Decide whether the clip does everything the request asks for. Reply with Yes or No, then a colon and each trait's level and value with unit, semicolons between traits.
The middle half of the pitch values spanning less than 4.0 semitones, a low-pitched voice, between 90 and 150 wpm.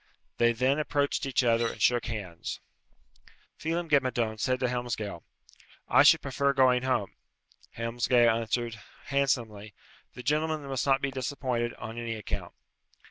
Yes: average, 2.9 semitones; low, 125 Hz; average, 140 wpm